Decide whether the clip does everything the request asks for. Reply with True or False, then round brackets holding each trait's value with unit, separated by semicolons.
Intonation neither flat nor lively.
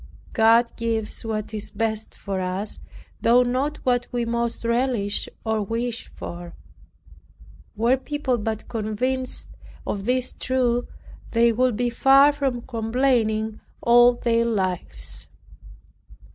False (2.3 semitones)